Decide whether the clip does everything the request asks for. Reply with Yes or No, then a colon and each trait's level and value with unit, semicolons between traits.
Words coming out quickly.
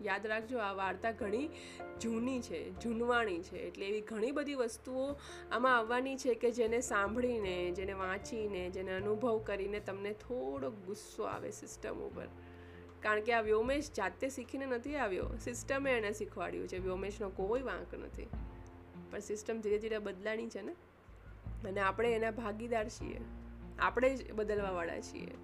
Yes: fast, 150 wpm